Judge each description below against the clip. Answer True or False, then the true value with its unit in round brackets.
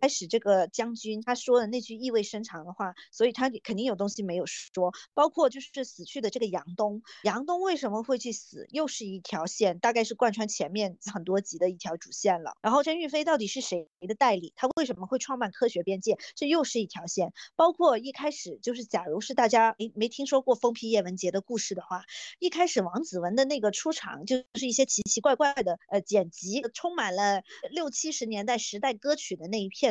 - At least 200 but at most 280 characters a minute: False (325 characters per minute)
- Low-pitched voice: False (230 Hz)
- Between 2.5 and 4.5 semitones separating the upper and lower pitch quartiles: False (4.9 semitones)